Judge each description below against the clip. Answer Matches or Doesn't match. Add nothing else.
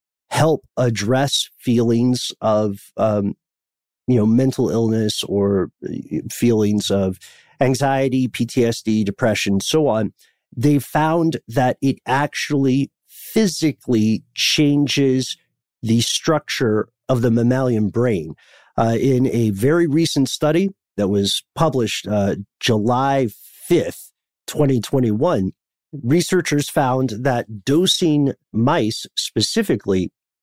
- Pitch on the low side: Matches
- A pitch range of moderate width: Matches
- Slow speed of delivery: Matches